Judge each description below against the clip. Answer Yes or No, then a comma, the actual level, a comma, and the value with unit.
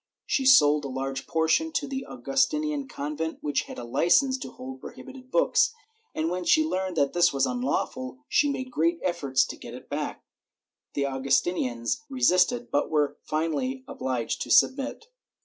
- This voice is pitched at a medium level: Yes, medium, 175 Hz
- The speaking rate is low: No, average, 165 wpm